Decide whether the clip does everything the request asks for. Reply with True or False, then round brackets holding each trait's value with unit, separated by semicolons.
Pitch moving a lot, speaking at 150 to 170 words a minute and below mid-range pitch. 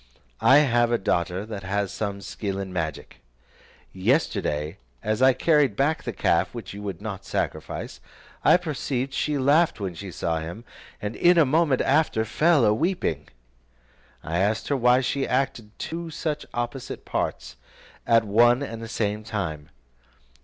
True (5.9 semitones; 160 wpm; 115 Hz)